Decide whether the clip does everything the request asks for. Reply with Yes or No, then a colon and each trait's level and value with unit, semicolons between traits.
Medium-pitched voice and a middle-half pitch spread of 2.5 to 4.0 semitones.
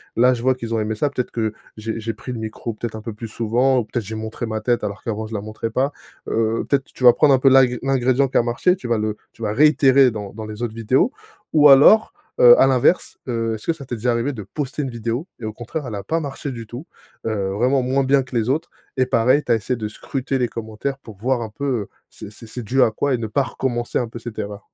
No: low, 120 Hz; average, 3.3 semitones